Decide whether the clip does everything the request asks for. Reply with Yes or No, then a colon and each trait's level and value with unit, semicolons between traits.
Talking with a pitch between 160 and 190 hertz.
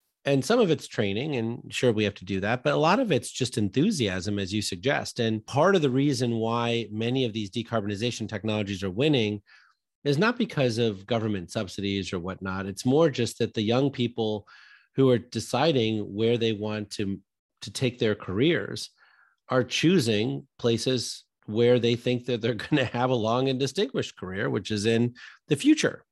No: low, 115 Hz